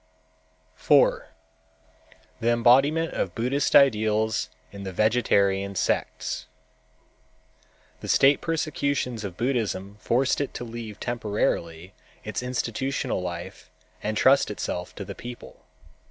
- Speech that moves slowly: Yes, slow, 110 wpm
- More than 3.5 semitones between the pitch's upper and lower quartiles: Yes, average, 4.6 semitones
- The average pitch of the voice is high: No, low, 115 Hz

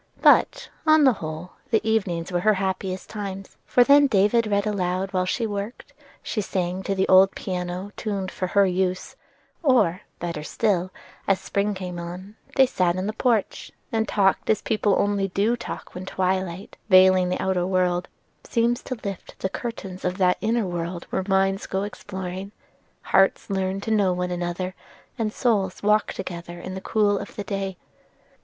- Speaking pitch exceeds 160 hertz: Yes, high, 190 Hz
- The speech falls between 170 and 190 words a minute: Yes, average, 175 wpm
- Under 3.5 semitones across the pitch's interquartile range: Yes, narrow, 2.4 semitones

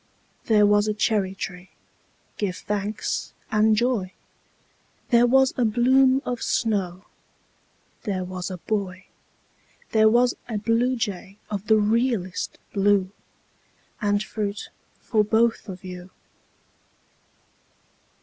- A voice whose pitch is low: No, high, 210 Hz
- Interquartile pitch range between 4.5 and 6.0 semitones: No, average, 3.2 semitones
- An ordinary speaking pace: No, slow, 110 wpm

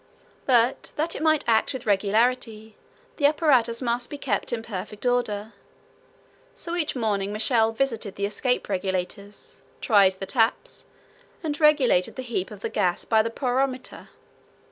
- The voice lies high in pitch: Yes, high, 230 Hz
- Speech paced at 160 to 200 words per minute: No, average, 145 wpm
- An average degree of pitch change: Yes, average, 4.0 semitones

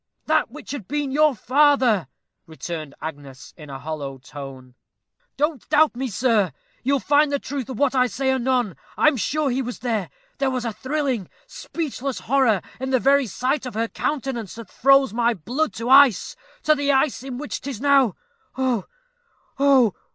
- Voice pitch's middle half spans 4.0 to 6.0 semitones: Yes, average, 4.3 semitones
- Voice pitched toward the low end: No, very high, 260 Hz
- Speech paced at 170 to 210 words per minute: Yes, average, 180 wpm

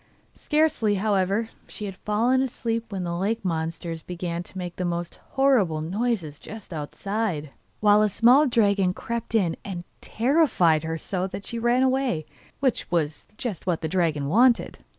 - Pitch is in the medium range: No, high, 195 Hz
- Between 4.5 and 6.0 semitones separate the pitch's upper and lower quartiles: Yes, average, 5.3 semitones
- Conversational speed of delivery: Yes, average, 160 wpm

